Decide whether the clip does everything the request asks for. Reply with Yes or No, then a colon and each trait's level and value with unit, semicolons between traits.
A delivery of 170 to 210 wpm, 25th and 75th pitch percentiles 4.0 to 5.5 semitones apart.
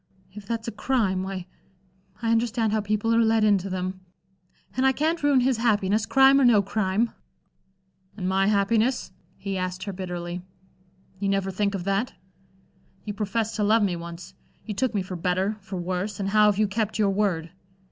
No: average, 185 wpm; average, 3.0 semitones